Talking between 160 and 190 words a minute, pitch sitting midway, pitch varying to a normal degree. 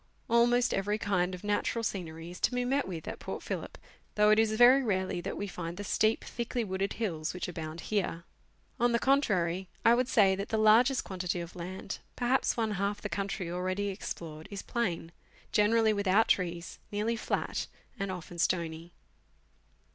No: average, 175 wpm; high, 200 Hz; average, 4.0 semitones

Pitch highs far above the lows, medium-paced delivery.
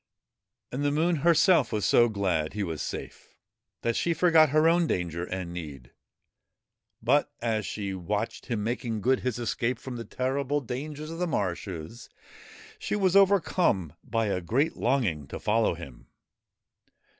Yes: wide, 7.8 semitones; average, 155 wpm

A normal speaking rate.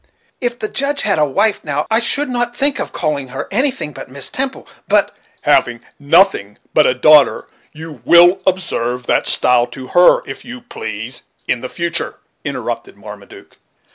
Yes: average, 165 wpm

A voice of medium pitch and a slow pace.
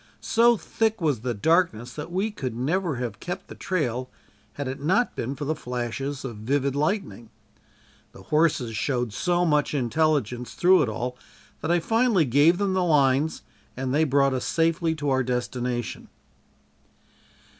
No: medium, 145 Hz; average, 160 wpm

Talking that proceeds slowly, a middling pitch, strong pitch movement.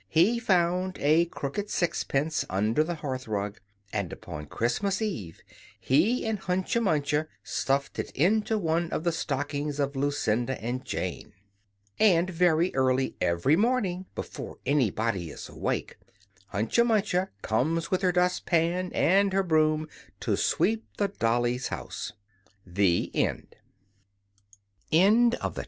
Yes: slow, 130 wpm; medium, 155 Hz; wide, 7.6 semitones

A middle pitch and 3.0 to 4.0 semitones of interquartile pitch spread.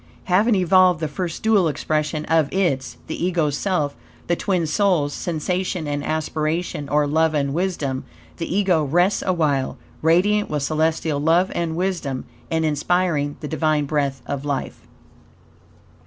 Yes: medium, 160 Hz; average, 3.5 semitones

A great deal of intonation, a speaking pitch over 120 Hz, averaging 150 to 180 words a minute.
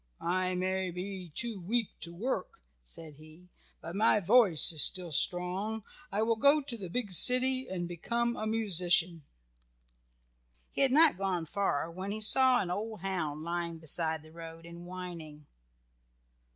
No: average, 4.7 semitones; medium, 185 Hz; average, 155 wpm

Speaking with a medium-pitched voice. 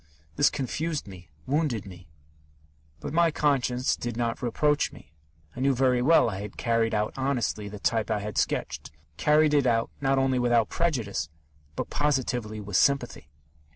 No: low, 120 Hz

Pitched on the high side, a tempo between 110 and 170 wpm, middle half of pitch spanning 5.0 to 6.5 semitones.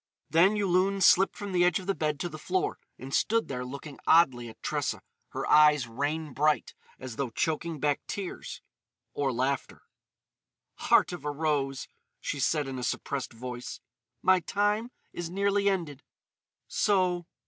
No: medium, 155 Hz; average, 155 wpm; average, 5.3 semitones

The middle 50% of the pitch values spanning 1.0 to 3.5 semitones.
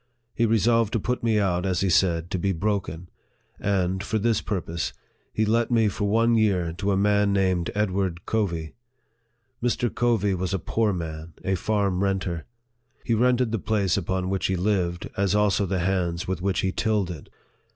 Yes: average, 3.2 semitones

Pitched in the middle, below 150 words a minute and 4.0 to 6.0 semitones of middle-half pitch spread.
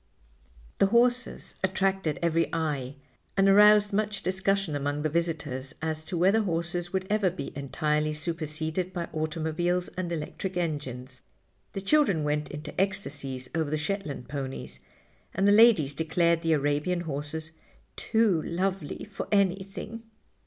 Yes: medium, 170 Hz; slow, 135 wpm; average, 4.4 semitones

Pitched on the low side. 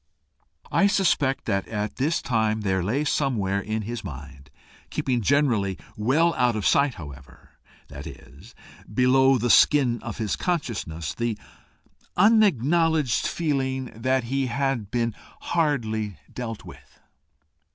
Yes: low, 120 Hz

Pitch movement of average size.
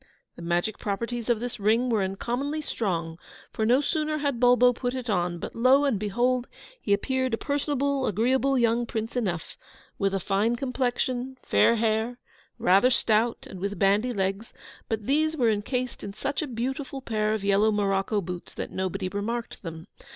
Yes: average, 4.1 semitones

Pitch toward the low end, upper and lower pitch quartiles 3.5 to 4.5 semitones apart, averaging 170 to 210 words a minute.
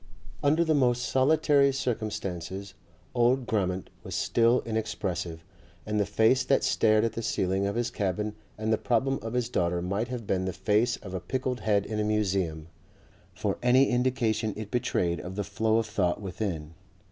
Yes: low, 110 Hz; average, 4.2 semitones; average, 175 wpm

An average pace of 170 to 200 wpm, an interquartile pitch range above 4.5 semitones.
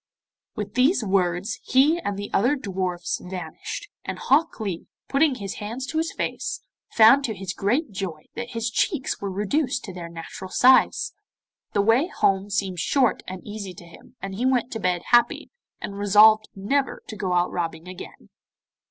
Yes: average, 175 wpm; average, 5.2 semitones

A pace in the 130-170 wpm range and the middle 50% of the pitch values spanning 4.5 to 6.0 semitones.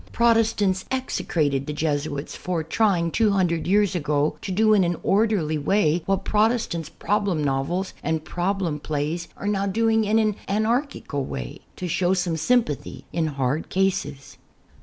Yes: average, 155 wpm; average, 5.3 semitones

